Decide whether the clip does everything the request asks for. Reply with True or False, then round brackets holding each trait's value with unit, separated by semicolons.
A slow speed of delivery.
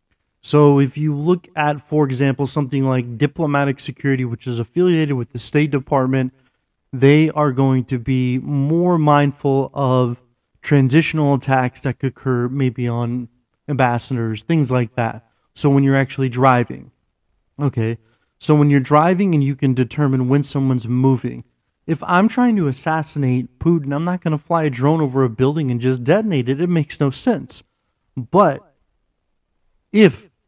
False (160 wpm)